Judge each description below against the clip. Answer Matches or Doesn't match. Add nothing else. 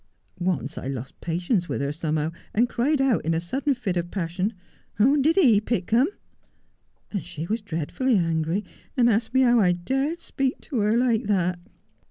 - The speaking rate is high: Doesn't match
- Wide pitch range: Matches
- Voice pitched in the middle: Doesn't match